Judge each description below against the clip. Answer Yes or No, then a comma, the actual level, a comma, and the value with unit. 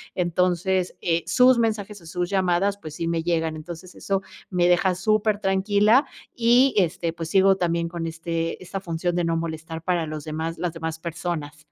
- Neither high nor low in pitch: Yes, medium, 175 Hz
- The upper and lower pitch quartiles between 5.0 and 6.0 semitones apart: No, average, 2.7 semitones